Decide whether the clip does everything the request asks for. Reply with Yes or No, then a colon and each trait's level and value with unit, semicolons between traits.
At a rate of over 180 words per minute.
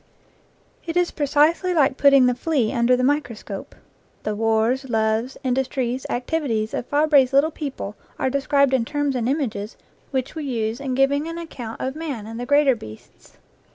No: average, 175 wpm